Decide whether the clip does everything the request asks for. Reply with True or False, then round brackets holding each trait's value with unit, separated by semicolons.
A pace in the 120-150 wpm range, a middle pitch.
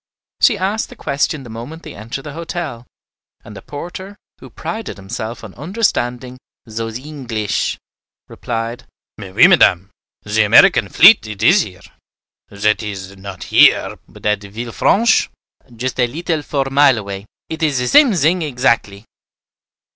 False (145 wpm; 125 Hz)